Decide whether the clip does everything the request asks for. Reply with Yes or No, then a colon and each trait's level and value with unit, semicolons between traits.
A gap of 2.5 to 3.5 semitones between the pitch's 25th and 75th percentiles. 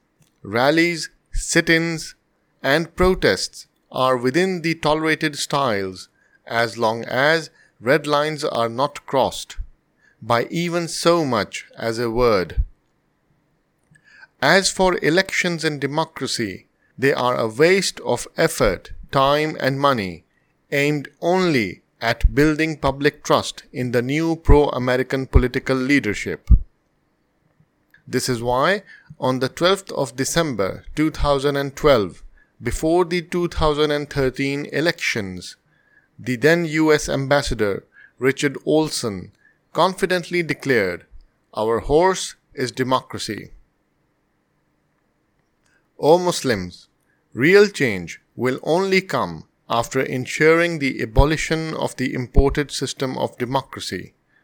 No: average, 4.2 semitones